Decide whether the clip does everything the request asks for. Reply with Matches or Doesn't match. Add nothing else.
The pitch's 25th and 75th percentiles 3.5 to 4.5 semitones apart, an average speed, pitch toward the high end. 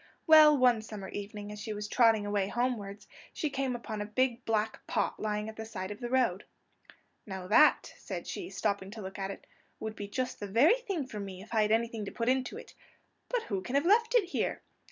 Doesn't match